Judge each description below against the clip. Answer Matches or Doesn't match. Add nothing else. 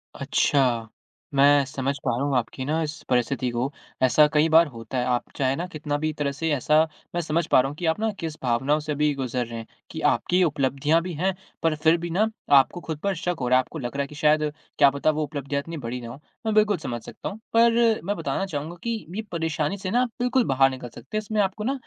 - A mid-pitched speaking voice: Matches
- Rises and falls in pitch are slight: Doesn't match